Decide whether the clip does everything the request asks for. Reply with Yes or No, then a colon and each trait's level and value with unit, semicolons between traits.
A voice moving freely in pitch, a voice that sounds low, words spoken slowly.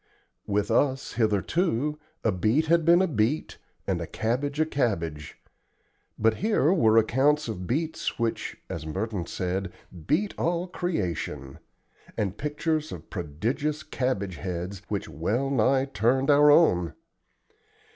Yes: wide, 7.5 semitones; low, 120 Hz; slow, 130 wpm